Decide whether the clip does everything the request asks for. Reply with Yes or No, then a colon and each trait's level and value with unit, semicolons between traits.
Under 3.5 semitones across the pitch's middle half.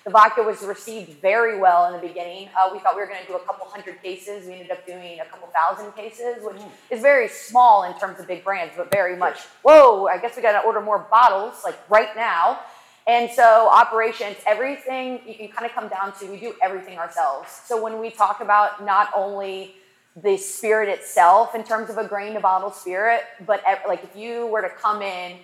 Yes: average, 3.0 semitones